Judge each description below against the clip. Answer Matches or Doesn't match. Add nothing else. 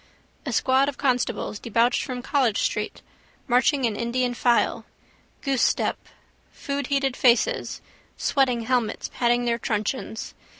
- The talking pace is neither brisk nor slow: Doesn't match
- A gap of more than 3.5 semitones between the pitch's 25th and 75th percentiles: Doesn't match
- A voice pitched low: Doesn't match